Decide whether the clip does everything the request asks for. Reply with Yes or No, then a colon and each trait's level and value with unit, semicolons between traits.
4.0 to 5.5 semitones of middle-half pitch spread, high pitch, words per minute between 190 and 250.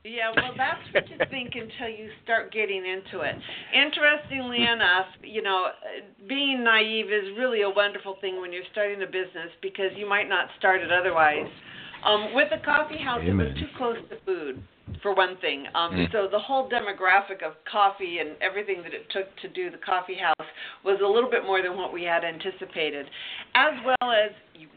Yes: average, 4.3 semitones; high, 205 Hz; average, 195 wpm